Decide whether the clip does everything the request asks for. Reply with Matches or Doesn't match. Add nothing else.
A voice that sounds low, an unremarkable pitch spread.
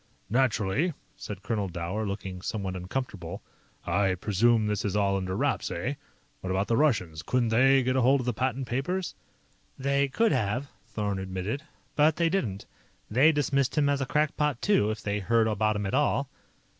Doesn't match